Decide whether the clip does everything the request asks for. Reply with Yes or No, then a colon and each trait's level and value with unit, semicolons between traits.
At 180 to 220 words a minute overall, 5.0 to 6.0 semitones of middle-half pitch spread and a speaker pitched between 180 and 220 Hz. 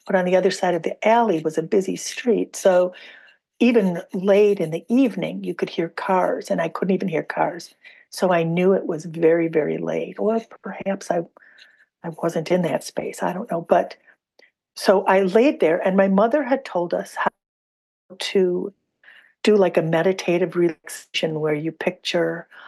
No: average, 185 wpm; average, 3.7 semitones; medium, 185 Hz